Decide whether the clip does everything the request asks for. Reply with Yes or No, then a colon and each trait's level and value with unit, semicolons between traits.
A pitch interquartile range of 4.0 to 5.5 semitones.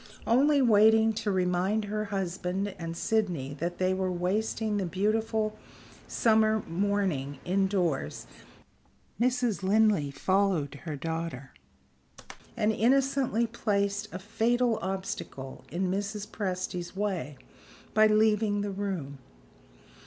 No: average, 3.4 semitones